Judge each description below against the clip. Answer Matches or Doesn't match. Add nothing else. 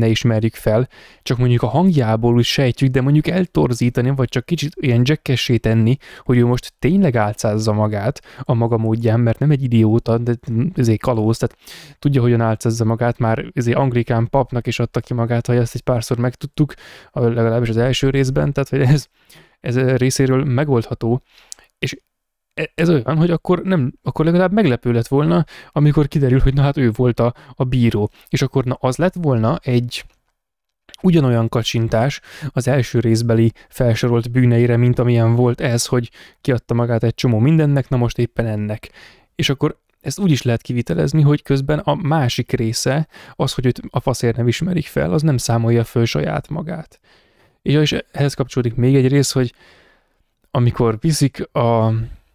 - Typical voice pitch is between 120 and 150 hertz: Matches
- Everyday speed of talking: Doesn't match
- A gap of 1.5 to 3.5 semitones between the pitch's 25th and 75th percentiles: Matches